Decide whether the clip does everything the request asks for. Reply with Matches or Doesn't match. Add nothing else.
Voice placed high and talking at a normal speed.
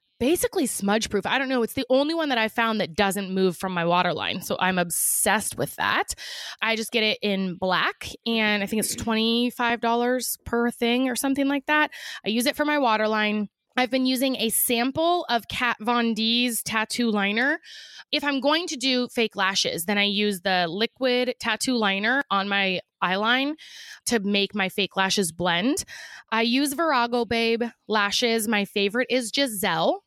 Matches